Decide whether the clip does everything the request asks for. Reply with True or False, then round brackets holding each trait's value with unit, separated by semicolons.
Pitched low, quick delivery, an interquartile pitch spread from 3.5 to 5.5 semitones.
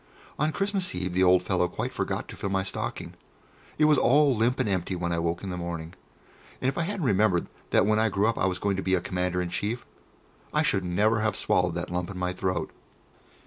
True (95 Hz; 235 wpm; 3.9 semitones)